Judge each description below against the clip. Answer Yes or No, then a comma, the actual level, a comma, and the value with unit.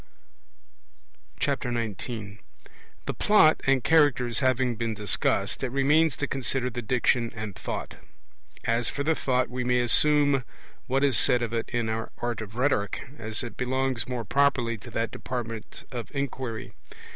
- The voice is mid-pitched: No, low, 125 Hz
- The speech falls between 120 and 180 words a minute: Yes, average, 150 wpm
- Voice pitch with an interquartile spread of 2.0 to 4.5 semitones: Yes, average, 2.8 semitones